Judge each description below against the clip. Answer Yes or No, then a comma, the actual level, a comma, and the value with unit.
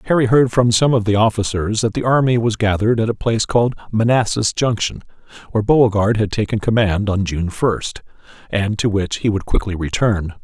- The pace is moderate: Yes, average, 190 wpm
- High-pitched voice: No, low, 110 Hz